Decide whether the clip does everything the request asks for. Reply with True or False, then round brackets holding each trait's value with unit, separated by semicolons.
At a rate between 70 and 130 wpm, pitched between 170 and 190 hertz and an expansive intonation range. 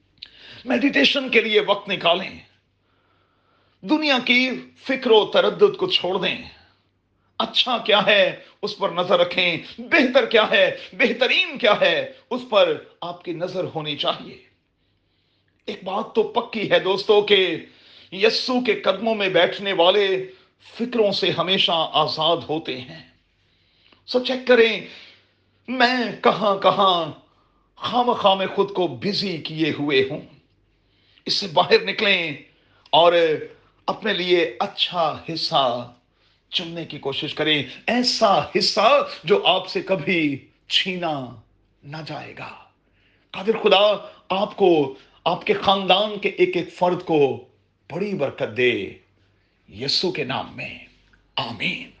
True (125 wpm; 185 Hz; 7.2 semitones)